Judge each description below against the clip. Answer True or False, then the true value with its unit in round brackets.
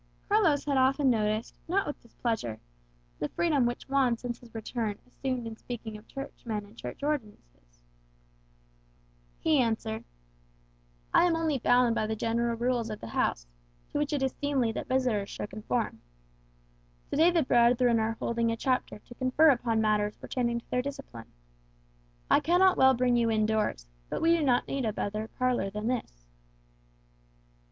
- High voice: True (240 Hz)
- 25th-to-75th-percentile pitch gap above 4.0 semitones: False (3.6 semitones)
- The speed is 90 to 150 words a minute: False (165 wpm)